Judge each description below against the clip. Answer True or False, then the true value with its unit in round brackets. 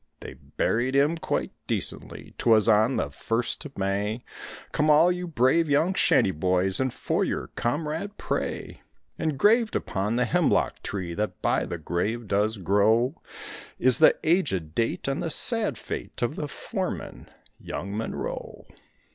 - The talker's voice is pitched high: False (120 Hz)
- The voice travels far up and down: True (7.4 semitones)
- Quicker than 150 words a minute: False (145 wpm)